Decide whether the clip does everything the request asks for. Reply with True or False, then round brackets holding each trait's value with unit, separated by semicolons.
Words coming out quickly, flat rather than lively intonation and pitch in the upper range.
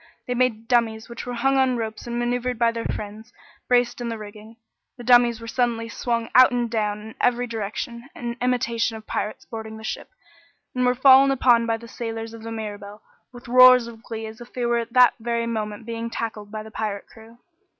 True (210 wpm; 1.7 semitones; 230 Hz)